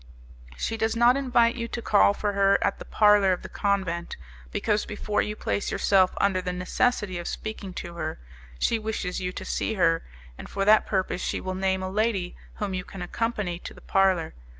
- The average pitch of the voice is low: No, high, 195 Hz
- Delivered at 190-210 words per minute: Yes, average, 200 wpm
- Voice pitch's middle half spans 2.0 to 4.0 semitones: Yes, average, 3.0 semitones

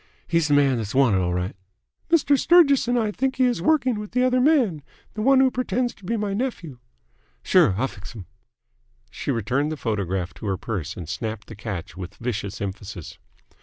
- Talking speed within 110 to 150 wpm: No, fast, 205 wpm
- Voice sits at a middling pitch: Yes, medium, 145 Hz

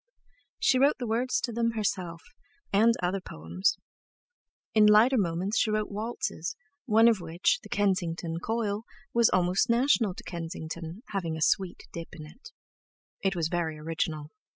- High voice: Yes, high, 195 Hz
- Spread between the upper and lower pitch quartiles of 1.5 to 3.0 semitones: No, average, 5.1 semitones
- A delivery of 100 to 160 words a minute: Yes, average, 155 wpm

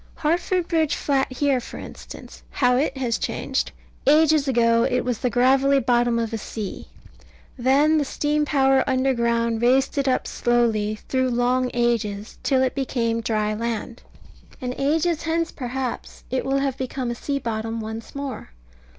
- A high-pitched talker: Yes, very high, 255 Hz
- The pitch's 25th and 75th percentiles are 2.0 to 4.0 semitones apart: Yes, average, 3.0 semitones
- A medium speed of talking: Yes, average, 160 wpm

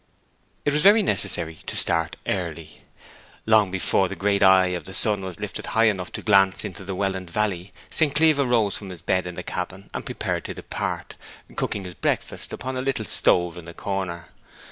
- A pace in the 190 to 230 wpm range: Yes, average, 195 wpm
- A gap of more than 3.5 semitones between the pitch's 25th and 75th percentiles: No, average, 3.2 semitones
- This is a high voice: No, very low, 95 Hz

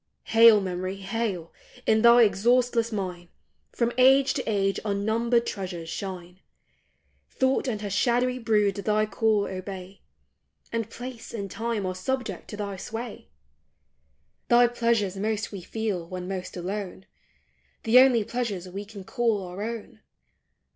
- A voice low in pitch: No, high, 210 Hz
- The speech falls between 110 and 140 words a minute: Yes, slow, 135 wpm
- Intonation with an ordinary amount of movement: Yes, average, 3.5 semitones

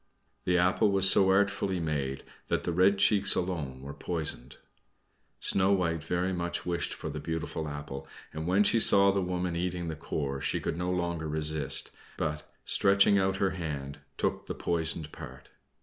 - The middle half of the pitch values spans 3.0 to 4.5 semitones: Yes, average, 3.6 semitones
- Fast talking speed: No, average, 170 wpm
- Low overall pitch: Yes, very low, 85 Hz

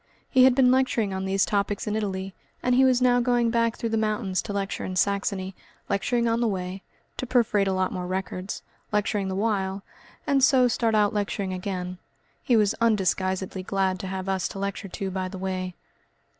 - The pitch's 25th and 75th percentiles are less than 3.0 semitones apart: No, average, 3.4 semitones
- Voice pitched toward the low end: No, high, 200 Hz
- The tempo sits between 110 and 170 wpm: No, average, 200 wpm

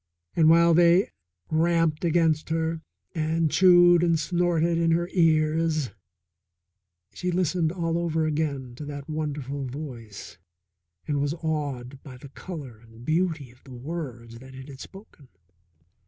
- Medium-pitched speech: Yes, medium, 155 Hz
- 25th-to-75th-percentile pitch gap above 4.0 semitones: No, average, 3.3 semitones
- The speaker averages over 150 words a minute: No, average, 140 wpm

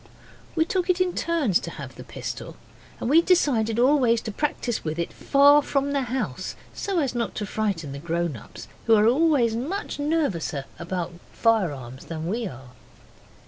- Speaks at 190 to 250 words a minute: No, average, 175 wpm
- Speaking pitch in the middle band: No, high, 230 Hz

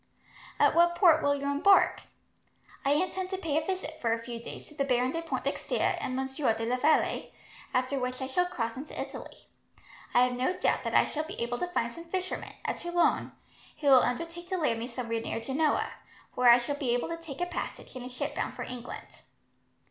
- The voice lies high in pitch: Yes, very high, 280 Hz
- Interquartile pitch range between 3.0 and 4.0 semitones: No, average, 5.2 semitones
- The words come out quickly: Yes, fast, 215 wpm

